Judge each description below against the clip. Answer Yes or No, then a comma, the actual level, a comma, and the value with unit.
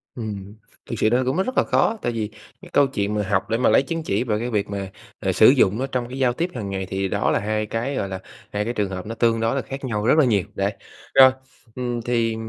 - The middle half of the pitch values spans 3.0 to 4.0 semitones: Yes, average, 3.7 semitones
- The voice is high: No, low, 115 Hz